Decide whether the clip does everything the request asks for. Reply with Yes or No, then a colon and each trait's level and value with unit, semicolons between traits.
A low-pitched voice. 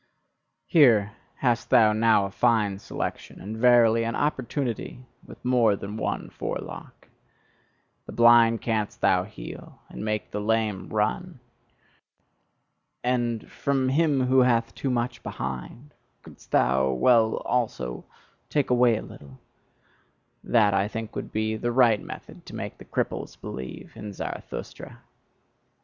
Yes: low, 115 Hz